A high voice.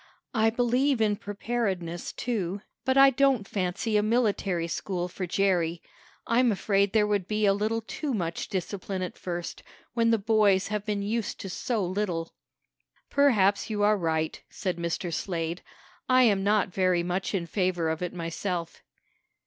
Yes: high, 200 Hz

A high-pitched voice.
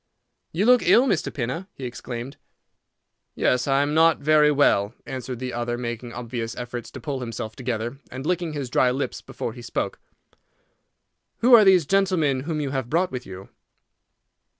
No: low, 130 Hz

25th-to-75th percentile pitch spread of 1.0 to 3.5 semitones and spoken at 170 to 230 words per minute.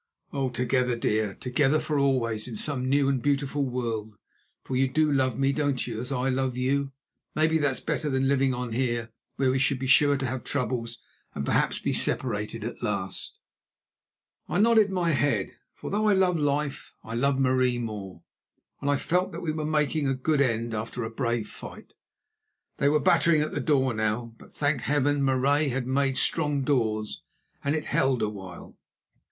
Yes: average, 3.2 semitones; average, 185 wpm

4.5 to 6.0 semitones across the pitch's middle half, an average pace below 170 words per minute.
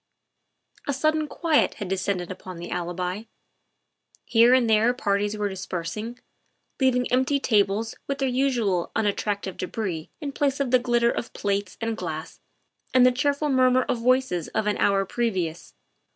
Yes: average, 5.0 semitones; average, 150 wpm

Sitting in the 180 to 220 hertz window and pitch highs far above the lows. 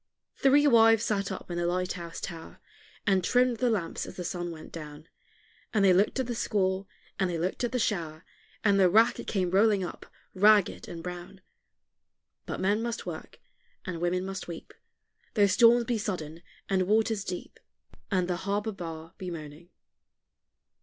No: high, 190 Hz; average, 3.7 semitones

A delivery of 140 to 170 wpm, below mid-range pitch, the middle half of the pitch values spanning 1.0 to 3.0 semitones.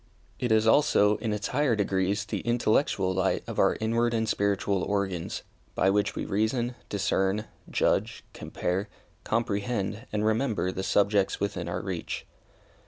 Yes: average, 145 wpm; low, 105 Hz; narrow, 2.6 semitones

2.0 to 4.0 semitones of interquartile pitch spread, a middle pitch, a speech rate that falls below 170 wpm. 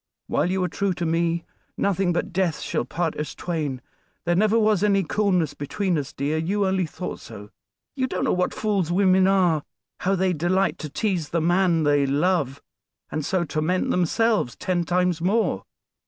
No: average, 3.3 semitones; medium, 180 Hz; average, 180 wpm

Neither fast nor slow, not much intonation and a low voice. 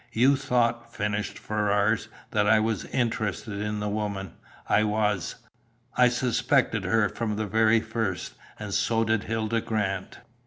Yes: average, 145 wpm; narrow, 1.6 semitones; low, 110 Hz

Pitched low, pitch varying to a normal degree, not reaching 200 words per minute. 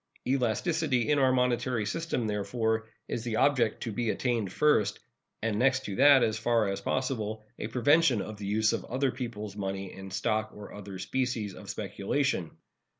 Yes: low, 115 Hz; average, 3.8 semitones; average, 170 wpm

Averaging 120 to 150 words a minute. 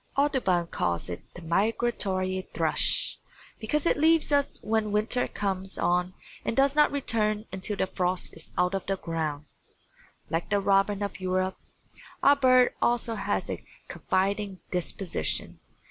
Yes: average, 145 wpm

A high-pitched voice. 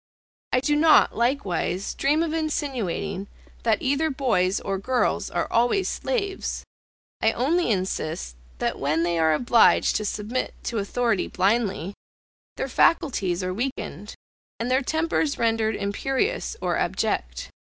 Yes: high, 235 Hz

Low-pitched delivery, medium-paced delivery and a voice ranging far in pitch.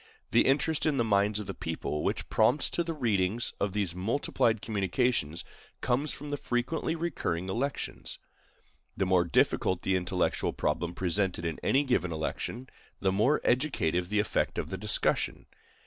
Yes: low, 105 Hz; average, 160 wpm; wide, 6.2 semitones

